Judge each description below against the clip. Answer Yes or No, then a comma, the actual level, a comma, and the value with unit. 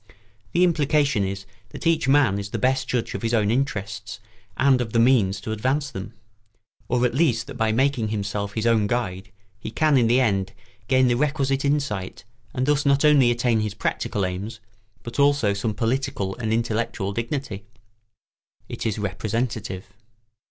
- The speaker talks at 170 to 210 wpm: Yes, average, 175 wpm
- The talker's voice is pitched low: Yes, low, 115 Hz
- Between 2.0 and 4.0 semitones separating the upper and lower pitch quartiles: No, average, 4.7 semitones